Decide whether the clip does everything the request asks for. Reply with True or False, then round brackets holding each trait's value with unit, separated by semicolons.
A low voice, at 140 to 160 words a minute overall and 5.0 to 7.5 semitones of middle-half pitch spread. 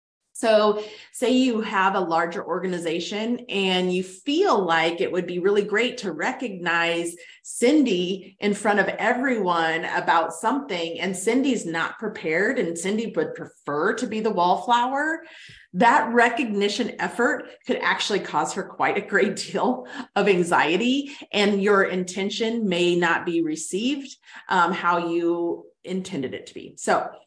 False (200 Hz; 145 wpm; 5.3 semitones)